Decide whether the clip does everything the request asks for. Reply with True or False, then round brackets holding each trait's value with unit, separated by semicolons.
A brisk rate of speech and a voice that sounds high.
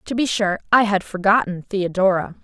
False (170 wpm; 200 Hz)